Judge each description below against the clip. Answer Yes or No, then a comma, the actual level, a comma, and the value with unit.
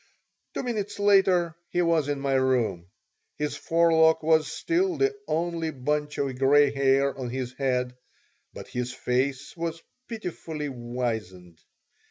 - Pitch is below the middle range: No, medium, 145 Hz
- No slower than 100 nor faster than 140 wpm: Yes, slow, 135 wpm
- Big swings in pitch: No, average, 4.6 semitones